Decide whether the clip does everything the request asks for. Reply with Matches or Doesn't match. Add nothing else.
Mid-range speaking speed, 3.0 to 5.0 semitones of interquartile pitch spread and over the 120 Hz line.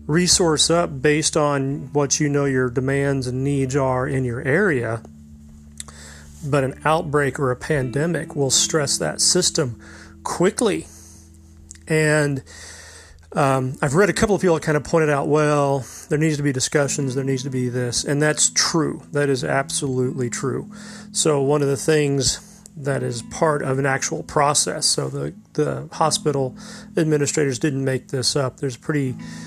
Matches